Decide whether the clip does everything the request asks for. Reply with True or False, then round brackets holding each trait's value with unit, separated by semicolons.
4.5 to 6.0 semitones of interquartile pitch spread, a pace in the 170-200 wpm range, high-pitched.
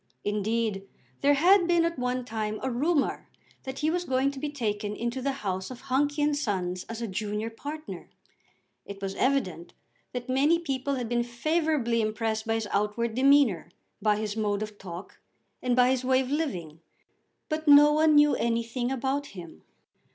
True (5.1 semitones; 175 wpm; 245 Hz)